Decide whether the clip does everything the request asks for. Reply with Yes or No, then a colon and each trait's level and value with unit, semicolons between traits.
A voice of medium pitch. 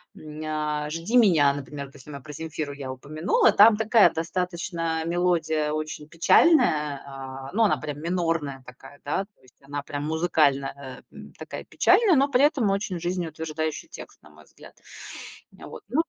Yes: medium, 155 Hz